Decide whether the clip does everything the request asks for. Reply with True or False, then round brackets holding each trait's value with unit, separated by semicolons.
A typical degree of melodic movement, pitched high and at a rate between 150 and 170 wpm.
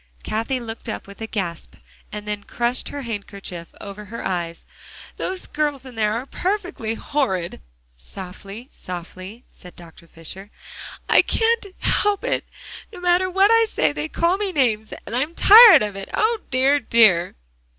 False (8.0 semitones; 225 Hz; 160 wpm)